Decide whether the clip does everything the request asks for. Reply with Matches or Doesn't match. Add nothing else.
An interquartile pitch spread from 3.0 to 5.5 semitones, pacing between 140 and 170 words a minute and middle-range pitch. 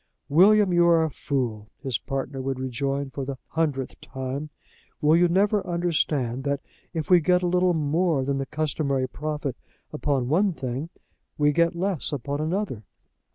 Matches